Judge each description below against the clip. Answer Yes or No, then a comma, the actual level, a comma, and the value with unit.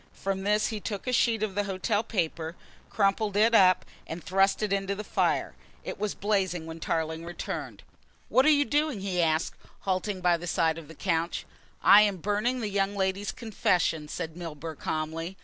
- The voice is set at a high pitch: Yes, high, 195 Hz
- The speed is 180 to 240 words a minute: Yes, average, 185 wpm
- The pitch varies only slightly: No, average, 3.9 semitones